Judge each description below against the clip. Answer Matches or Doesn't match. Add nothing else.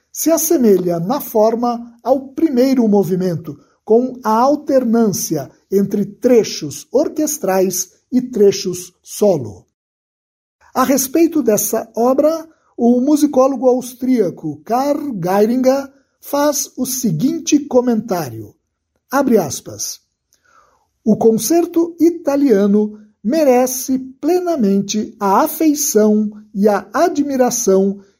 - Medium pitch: Doesn't match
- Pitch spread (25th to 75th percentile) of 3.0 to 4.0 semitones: Doesn't match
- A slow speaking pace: Matches